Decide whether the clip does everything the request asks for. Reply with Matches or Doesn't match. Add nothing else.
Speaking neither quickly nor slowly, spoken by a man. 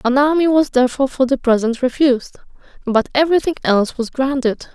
Doesn't match